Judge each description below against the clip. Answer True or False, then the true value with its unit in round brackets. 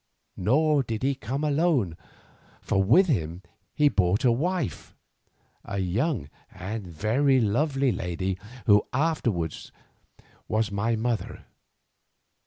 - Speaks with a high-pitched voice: False (115 Hz)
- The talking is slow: True (110 wpm)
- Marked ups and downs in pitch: True (6.4 semitones)